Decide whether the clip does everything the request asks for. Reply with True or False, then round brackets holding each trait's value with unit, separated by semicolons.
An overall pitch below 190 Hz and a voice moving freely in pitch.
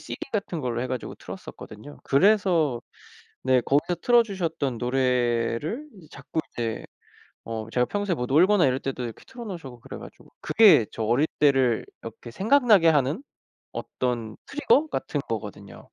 True (135 Hz; 7.7 semitones)